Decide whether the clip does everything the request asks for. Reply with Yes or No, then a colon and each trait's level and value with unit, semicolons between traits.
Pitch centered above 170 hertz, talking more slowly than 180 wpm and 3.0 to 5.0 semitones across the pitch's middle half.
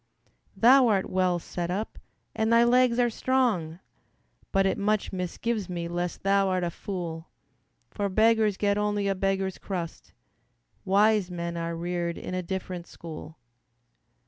Yes: high, 190 Hz; average, 145 wpm; average, 3.4 semitones